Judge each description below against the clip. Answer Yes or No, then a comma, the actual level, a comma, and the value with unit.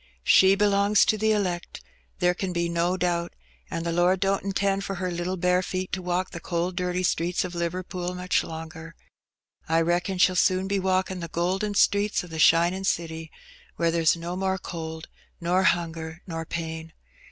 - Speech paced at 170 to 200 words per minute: Yes, average, 180 wpm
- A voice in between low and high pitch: Yes, medium, 180 Hz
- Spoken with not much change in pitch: Yes, narrow, 1.9 semitones